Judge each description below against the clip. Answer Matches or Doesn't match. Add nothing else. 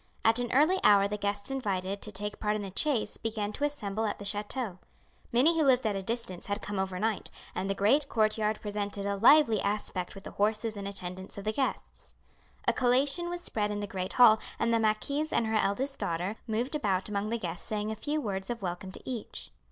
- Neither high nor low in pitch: Doesn't match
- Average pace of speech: Doesn't match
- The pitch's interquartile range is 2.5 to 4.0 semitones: Matches